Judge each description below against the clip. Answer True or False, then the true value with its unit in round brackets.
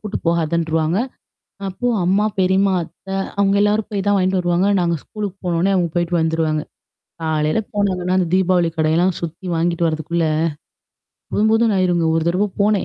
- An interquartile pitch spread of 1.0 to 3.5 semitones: True (2.8 semitones)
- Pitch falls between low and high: True (180 Hz)